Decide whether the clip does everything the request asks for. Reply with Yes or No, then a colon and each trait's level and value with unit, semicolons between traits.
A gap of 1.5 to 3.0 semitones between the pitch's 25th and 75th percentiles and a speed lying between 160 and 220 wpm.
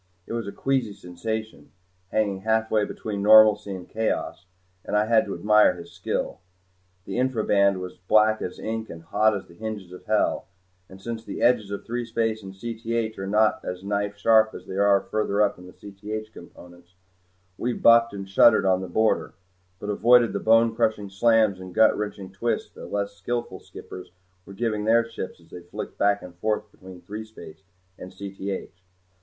Yes: narrow, 2.5 semitones; average, 185 wpm